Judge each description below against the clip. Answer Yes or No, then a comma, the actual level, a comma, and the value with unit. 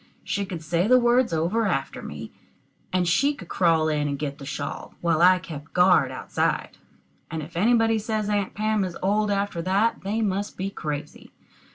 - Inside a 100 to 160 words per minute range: No, average, 185 wpm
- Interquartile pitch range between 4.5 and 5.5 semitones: Yes, average, 4.9 semitones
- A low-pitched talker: No, medium, 185 Hz